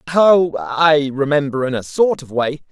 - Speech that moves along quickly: No, average, 175 wpm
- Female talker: No, male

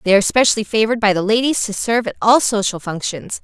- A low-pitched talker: No, high, 215 Hz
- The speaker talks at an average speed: No, fast, 225 wpm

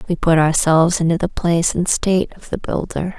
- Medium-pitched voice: Yes, medium, 170 Hz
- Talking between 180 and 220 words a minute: Yes, fast, 205 wpm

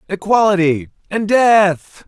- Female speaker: No, male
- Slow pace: Yes, slow, 85 wpm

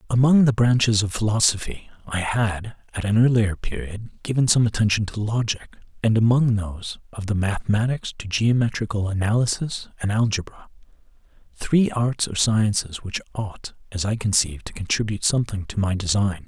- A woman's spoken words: No, male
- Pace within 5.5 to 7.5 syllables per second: No, 5.3 syllables/s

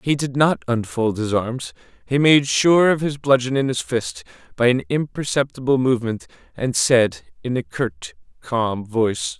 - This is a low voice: Yes, low, 130 Hz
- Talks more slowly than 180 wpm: Yes, average, 165 wpm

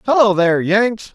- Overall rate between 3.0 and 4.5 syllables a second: No, 5.0 syllables/s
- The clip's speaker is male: Yes, male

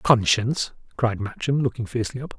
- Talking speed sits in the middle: Yes, average, 150 wpm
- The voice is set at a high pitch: No, low, 120 Hz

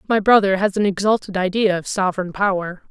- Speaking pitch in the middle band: No, high, 195 Hz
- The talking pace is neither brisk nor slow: Yes, average, 185 wpm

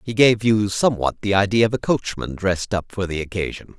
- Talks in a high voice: No, low, 100 Hz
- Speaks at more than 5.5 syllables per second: Yes, 5.8 syllables/s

